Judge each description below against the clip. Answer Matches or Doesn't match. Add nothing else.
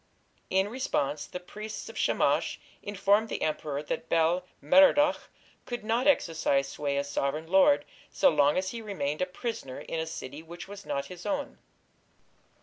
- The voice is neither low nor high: Matches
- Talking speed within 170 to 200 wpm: Doesn't match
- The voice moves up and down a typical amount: Doesn't match